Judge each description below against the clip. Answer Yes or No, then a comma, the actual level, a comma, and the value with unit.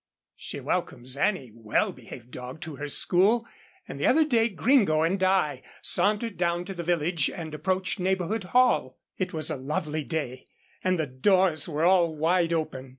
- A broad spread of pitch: No, average, 4.0 semitones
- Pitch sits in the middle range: Yes, medium, 170 Hz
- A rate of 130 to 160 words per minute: No, average, 170 wpm